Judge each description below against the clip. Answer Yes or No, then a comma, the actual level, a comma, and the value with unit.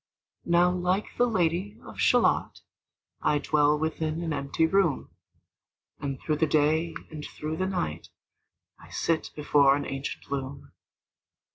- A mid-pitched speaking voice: Yes, medium, 155 Hz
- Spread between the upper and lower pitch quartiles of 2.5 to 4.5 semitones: Yes, average, 3.0 semitones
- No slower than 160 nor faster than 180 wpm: No, slow, 135 wpm